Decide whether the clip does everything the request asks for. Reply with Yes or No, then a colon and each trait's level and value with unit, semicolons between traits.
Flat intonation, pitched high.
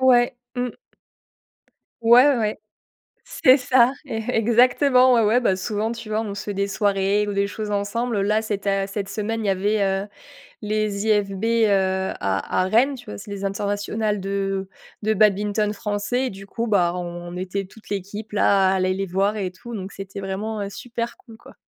Yes: narrow, 2.3 semitones; high, 205 Hz